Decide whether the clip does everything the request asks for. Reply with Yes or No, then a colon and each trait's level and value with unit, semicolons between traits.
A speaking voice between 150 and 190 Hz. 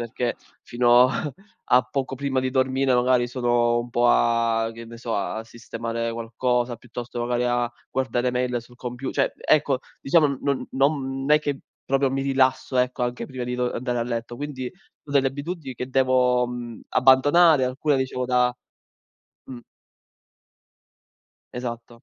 No: low, 125 Hz